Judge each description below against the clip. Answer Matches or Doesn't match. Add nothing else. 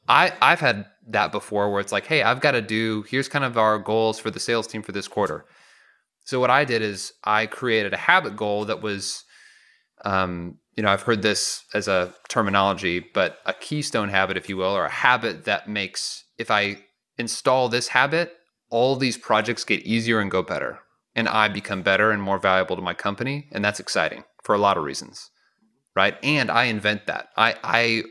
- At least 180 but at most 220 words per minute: Matches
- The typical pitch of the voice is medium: Doesn't match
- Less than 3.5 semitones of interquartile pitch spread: Matches